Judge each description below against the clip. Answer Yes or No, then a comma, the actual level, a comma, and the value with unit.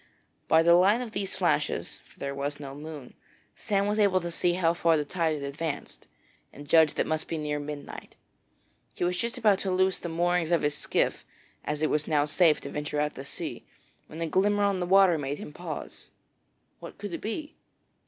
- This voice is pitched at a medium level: Yes, medium, 165 Hz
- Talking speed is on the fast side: Yes, fast, 210 wpm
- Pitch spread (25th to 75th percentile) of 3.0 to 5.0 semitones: Yes, average, 4.0 semitones